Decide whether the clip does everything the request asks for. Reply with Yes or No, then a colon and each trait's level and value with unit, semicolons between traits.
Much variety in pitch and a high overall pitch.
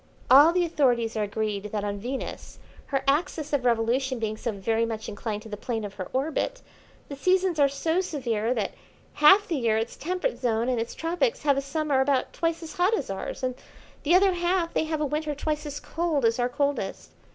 Yes: wide, 6.0 semitones; very high, 275 Hz